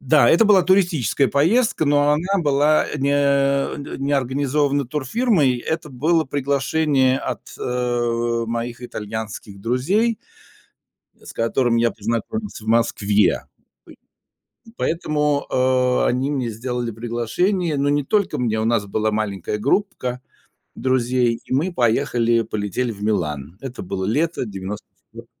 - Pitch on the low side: Yes, low, 130 Hz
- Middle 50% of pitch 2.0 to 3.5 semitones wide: No, average, 4.2 semitones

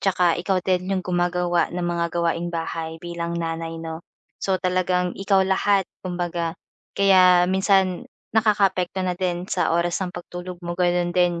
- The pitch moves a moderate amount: No, narrow, 1.4 semitones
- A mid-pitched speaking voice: Yes, medium, 180 Hz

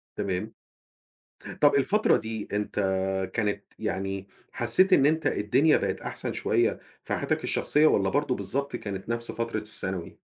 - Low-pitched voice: Yes, low, 115 Hz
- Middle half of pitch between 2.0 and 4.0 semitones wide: No, wide, 5.5 semitones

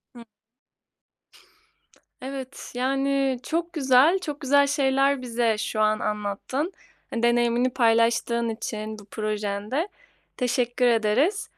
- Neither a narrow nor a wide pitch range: Yes, average, 3.6 semitones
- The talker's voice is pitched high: Yes, high, 245 Hz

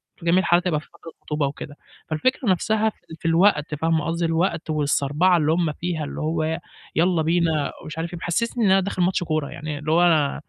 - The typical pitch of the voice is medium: Yes, medium, 165 Hz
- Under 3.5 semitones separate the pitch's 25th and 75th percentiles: Yes, narrow, 2.5 semitones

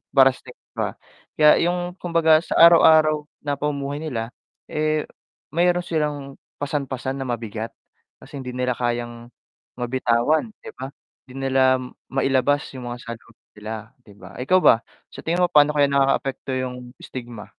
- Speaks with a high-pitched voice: No, low, 135 Hz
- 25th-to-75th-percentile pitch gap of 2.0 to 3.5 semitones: No, average, 3.9 semitones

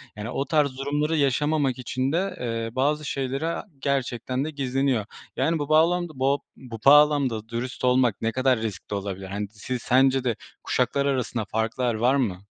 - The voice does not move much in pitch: No, average, 3.8 semitones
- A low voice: Yes, low, 130 Hz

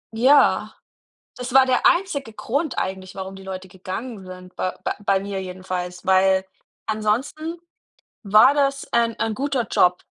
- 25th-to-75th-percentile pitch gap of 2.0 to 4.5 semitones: No, wide, 5.6 semitones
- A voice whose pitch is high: Yes, high, 210 Hz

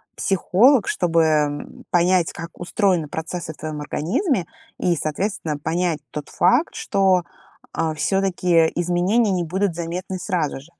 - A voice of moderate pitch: Yes, medium, 175 Hz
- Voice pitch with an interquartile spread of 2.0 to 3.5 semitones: Yes, average, 3.1 semitones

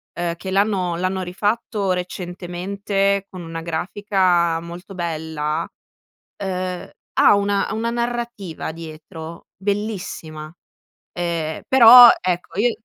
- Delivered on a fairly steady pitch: No, average, 3.1 semitones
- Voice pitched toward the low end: No, medium, 185 Hz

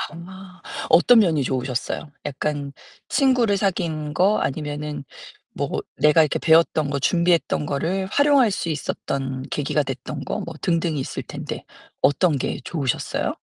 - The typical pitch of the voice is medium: Yes, medium, 155 Hz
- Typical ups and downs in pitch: Yes, average, 4.4 semitones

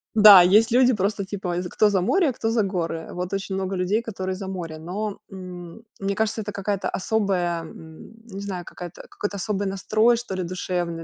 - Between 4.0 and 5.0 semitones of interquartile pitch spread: No, average, 2.8 semitones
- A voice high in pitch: Yes, high, 195 Hz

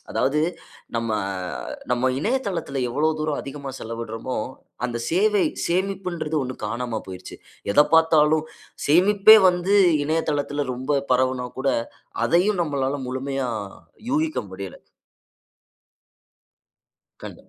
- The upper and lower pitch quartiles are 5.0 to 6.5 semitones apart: Yes, wide, 5.4 semitones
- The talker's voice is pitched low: No, medium, 145 Hz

